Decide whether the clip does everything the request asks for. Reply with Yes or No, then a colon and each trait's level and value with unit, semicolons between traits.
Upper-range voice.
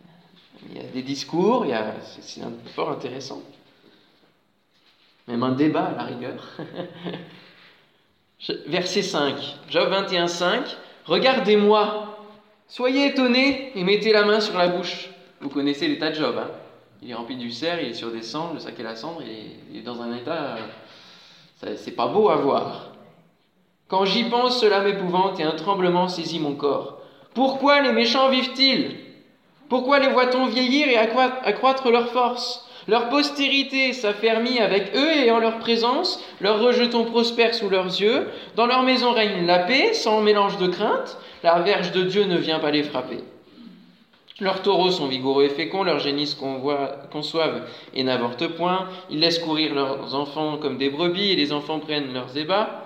Yes: high, 195 Hz